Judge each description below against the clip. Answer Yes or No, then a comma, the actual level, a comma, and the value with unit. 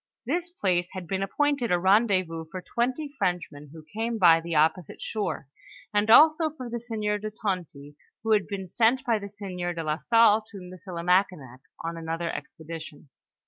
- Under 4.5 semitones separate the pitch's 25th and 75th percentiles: No, average, 5.0 semitones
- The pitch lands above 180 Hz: Yes, high, 190 Hz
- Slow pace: No, average, 175 wpm